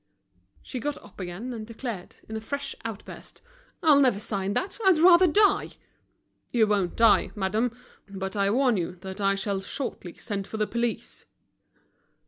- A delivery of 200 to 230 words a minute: No, average, 160 wpm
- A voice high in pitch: Yes, high, 220 Hz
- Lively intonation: No, average, 4.6 semitones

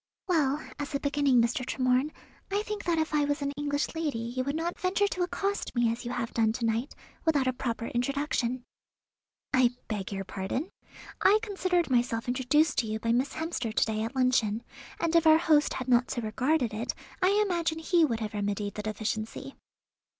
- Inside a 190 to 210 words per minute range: Yes, average, 195 wpm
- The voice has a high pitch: Yes, very high, 260 Hz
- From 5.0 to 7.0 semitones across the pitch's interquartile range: Yes, wide, 5.6 semitones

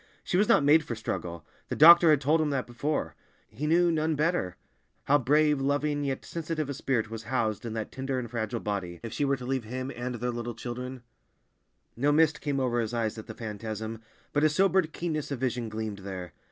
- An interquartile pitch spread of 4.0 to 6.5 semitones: Yes, average, 4.8 semitones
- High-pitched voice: No, low, 130 Hz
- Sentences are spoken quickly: Yes, fast, 215 wpm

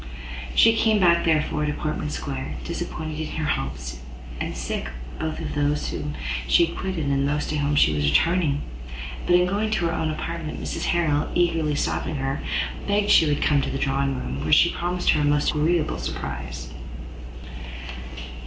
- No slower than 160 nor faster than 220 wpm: Yes, average, 180 wpm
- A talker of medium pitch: Yes, medium, 150 Hz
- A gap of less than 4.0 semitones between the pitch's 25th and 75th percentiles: Yes, average, 3.6 semitones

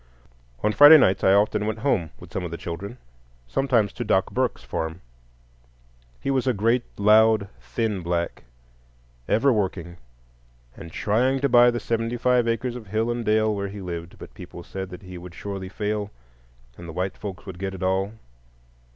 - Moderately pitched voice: No, low, 100 Hz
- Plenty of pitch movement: No, average, 4.1 semitones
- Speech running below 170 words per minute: No, average, 175 wpm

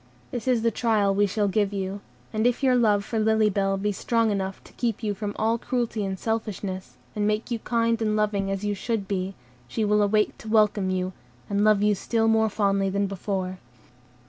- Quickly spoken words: Yes, fast, 210 wpm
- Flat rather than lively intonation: Yes, narrow, 2.2 semitones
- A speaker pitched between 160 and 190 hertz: No, high, 210 Hz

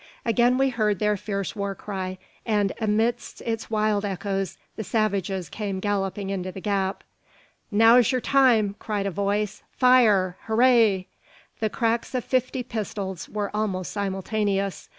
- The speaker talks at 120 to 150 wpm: Yes, average, 140 wpm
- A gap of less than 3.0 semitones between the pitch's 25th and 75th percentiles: Yes, narrow, 2.6 semitones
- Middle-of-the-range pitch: No, high, 210 Hz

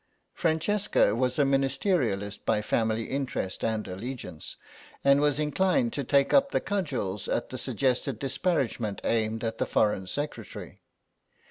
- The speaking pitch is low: Yes, low, 130 Hz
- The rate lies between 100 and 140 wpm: Yes, slow, 135 wpm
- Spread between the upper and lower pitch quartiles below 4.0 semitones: No, average, 5.3 semitones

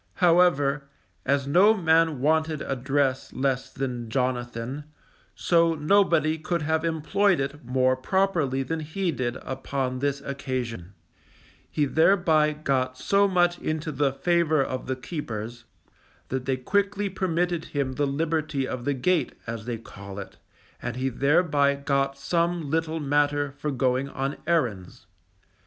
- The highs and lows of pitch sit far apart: No, average, 3.9 semitones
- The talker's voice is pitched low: No, medium, 145 Hz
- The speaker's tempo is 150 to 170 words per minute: No, average, 140 wpm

